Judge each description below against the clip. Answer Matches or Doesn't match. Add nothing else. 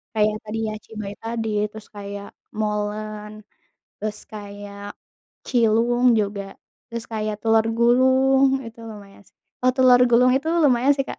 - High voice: Matches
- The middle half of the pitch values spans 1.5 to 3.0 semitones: Matches